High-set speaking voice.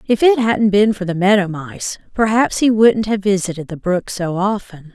Yes: high, 200 Hz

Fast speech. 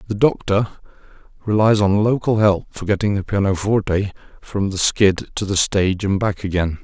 No: average, 165 wpm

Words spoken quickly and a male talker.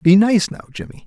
Yes: fast, 225 wpm; male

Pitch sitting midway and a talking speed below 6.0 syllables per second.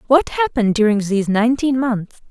No: high, 235 Hz; 5.8 syllables/s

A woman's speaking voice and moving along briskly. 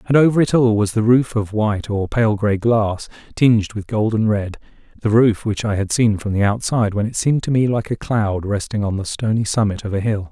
No: male; fast, 240 wpm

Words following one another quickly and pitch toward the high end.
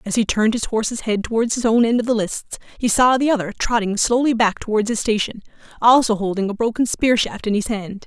Yes: fast, 240 wpm; high, 225 Hz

